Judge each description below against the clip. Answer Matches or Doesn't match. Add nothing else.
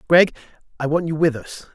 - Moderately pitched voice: Matches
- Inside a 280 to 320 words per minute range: Doesn't match